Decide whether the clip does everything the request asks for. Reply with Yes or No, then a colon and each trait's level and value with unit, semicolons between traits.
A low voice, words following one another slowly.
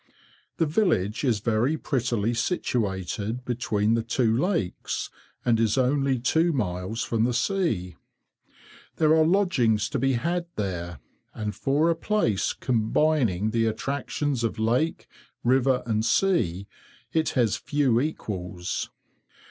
Yes: low, 120 Hz; slow, 125 wpm